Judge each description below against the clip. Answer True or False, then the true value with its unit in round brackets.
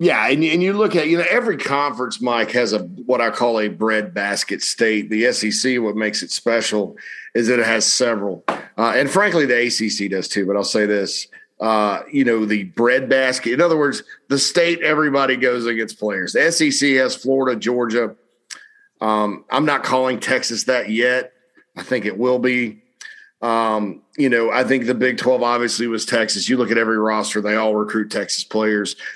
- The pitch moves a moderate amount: True (3.7 semitones)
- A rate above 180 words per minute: True (190 wpm)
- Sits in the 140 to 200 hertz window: False (120 Hz)